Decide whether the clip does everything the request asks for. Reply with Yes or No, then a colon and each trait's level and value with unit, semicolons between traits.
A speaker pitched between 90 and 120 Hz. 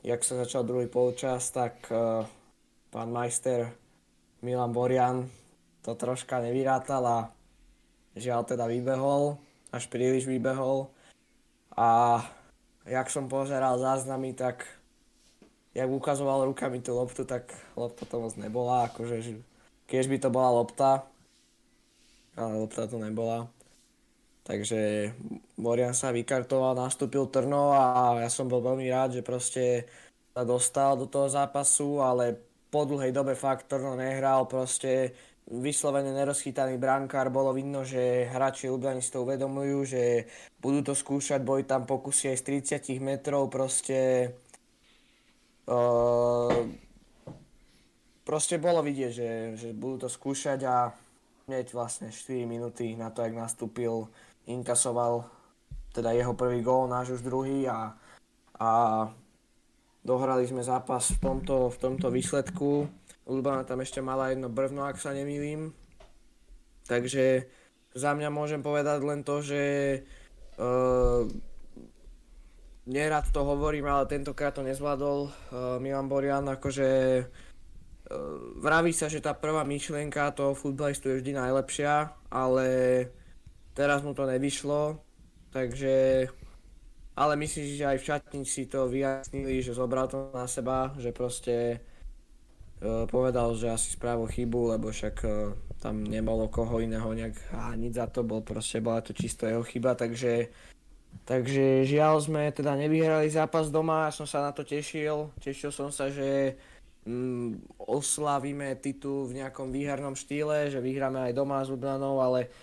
No: low, 130 Hz